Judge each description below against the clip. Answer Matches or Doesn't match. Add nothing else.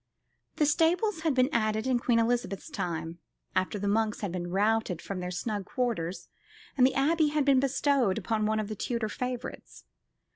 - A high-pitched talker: Matches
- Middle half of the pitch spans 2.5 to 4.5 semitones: Doesn't match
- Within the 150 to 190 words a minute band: Matches